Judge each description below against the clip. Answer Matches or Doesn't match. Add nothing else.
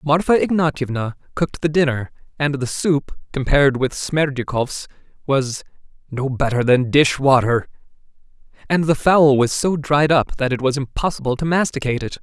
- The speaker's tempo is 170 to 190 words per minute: Doesn't match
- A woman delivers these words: Doesn't match